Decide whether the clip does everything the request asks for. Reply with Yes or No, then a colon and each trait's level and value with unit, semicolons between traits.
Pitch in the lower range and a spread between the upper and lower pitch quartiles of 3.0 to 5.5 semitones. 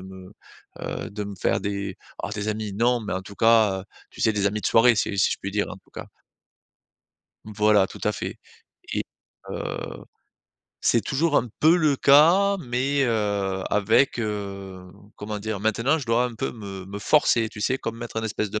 Yes: low, 105 Hz; average, 3.3 semitones